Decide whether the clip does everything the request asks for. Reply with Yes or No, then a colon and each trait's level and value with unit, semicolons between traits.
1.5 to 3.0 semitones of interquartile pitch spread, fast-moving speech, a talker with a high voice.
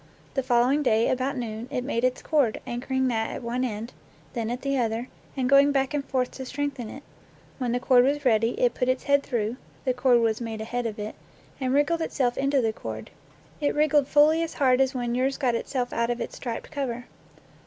Yes: narrow, 2.6 semitones; fast, 220 wpm; very high, 255 Hz